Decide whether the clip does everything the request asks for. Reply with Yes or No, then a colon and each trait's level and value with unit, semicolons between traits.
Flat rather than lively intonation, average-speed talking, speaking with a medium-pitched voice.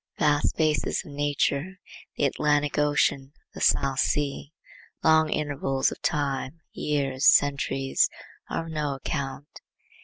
No: narrow, 1.5 semitones; slow, 120 wpm; medium, 145 Hz